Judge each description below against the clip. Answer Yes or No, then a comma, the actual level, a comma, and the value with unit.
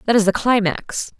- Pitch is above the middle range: Yes, high, 210 Hz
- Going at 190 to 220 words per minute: Yes, average, 200 wpm